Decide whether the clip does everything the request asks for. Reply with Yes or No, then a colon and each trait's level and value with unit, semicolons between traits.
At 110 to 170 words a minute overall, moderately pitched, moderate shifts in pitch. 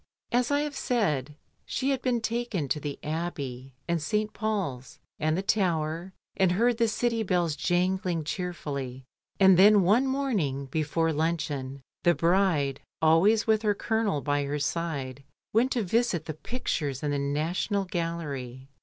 No: average, 155 wpm; medium, 170 Hz; wide, 6.6 semitones